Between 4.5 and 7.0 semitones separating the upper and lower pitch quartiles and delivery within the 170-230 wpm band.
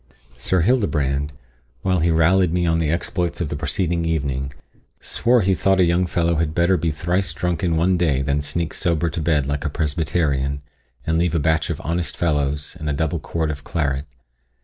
No: average, 2.9 semitones; average, 195 wpm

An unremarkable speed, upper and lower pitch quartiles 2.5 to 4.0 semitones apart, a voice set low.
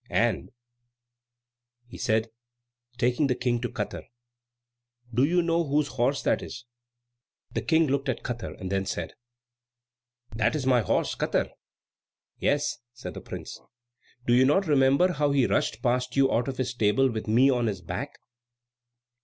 Yes: average, 155 wpm; average, 3.0 semitones; low, 125 Hz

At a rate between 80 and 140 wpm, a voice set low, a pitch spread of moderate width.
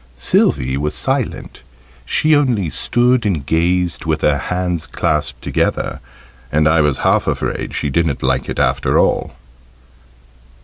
Yes: slow, 135 wpm; very low, 80 Hz; average, 4.2 semitones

